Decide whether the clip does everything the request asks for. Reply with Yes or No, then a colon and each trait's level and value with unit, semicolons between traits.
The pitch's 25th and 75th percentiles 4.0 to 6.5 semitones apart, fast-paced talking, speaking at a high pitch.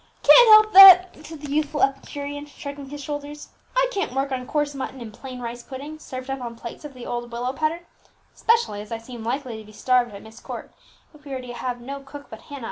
No: average, 3.4 semitones; fast, 230 wpm; very high, 275 Hz